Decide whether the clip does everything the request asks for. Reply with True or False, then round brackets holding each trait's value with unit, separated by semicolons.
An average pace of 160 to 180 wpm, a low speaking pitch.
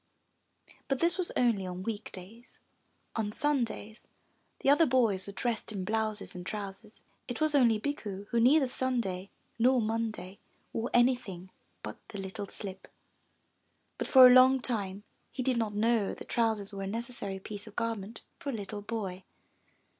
False (165 wpm; 220 Hz)